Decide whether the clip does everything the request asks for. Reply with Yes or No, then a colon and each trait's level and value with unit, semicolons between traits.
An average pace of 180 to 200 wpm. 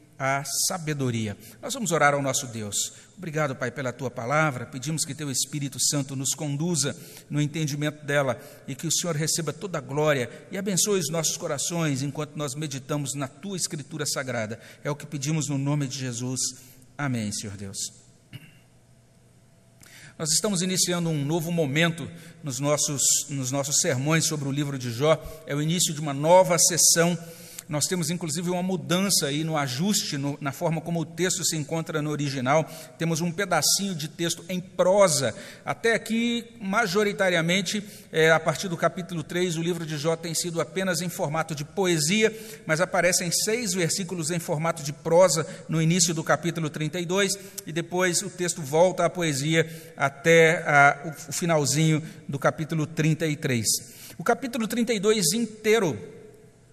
No: average, 160 wpm